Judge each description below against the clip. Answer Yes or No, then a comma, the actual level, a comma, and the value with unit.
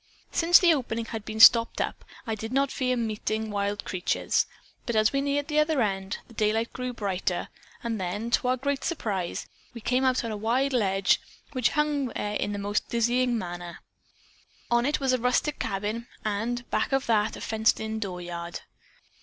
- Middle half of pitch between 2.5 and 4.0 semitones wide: Yes, average, 3.6 semitones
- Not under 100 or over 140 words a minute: No, average, 185 wpm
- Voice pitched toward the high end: Yes, high, 225 Hz